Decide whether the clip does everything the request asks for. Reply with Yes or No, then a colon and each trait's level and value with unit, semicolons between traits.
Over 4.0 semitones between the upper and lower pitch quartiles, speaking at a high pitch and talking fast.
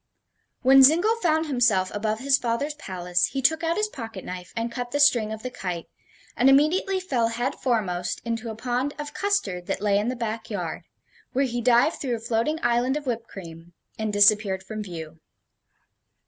No: average, 4.9 semitones; high, 235 Hz; average, 190 wpm